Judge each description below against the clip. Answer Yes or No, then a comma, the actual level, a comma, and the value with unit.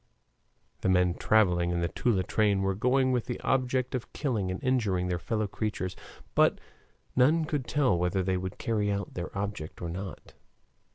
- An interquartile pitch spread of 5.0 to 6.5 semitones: Yes, average, 5.3 semitones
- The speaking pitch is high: No, low, 100 Hz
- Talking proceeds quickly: No, average, 175 wpm